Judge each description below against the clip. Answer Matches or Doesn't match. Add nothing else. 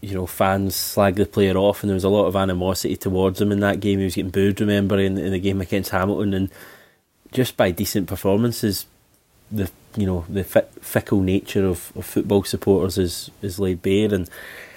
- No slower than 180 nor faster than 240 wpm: Matches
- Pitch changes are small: Matches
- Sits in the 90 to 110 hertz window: Matches